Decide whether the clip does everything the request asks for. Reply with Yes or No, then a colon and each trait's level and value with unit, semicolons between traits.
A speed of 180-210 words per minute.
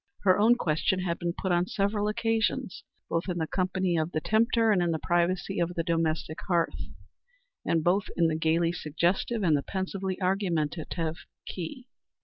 No: average, 170 wpm